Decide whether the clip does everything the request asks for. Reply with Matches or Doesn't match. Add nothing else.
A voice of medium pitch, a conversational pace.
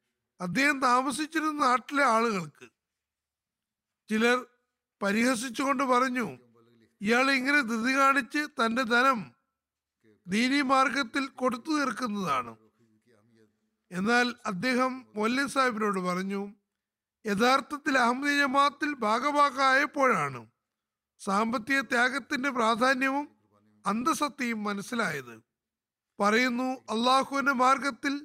Doesn't match